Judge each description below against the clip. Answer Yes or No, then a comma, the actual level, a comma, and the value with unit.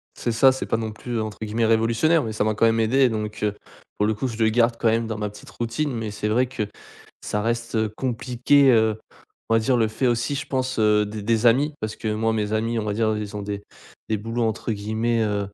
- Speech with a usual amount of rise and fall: No, narrow, 1.7 semitones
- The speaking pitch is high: No, low, 110 Hz